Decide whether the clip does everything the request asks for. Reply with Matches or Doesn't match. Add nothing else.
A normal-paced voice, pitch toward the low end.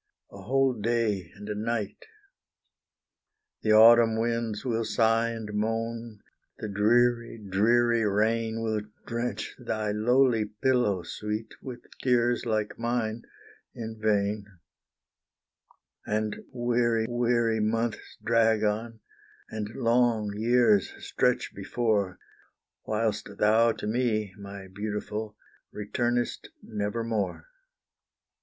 Doesn't match